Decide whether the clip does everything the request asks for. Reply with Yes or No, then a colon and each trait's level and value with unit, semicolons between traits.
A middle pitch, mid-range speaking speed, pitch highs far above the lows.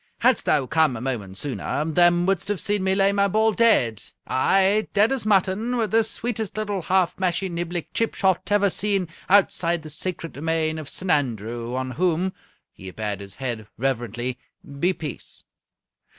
Yes: medium, 175 Hz; average, 165 wpm; wide, 7.1 semitones